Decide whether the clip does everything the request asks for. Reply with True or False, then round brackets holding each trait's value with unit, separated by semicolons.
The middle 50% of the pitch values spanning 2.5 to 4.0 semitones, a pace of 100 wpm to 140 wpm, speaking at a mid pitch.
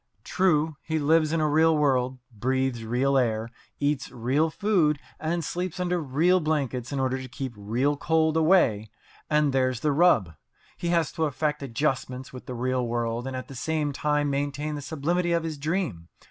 False (3.7 semitones; 180 wpm; 145 Hz)